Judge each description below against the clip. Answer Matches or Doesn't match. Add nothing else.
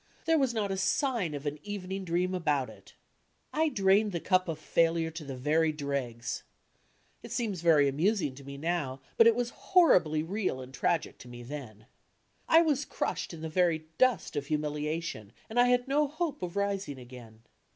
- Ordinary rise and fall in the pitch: Doesn't match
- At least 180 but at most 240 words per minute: Matches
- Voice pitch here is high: Doesn't match